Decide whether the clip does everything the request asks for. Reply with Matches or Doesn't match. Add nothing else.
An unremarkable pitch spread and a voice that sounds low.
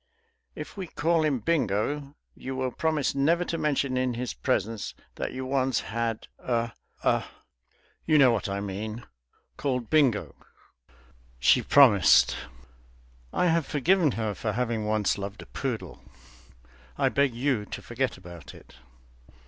Matches